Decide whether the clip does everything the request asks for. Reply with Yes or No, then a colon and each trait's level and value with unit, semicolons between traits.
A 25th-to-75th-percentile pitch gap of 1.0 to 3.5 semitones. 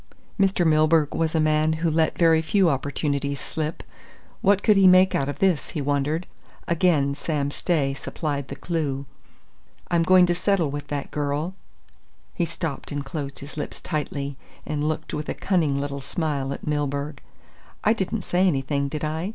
Yes: average, 3.1 semitones